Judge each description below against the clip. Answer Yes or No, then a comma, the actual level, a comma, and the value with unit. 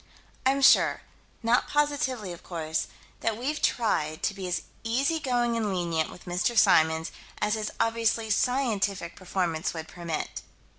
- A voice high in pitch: Yes, high, 210 Hz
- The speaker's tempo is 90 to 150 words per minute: Yes, average, 140 wpm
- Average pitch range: No, wide, 5.8 semitones